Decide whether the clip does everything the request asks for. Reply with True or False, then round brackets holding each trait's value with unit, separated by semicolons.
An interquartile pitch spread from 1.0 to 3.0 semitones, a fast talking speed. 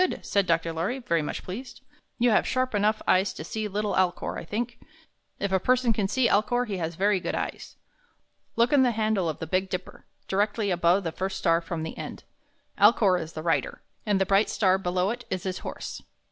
False (3.6 semitones; 210 wpm)